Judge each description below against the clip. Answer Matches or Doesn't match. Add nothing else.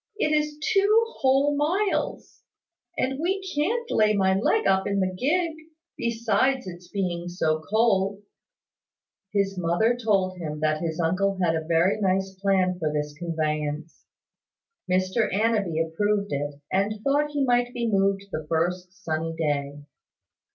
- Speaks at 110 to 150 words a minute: Matches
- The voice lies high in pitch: Matches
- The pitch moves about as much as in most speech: Doesn't match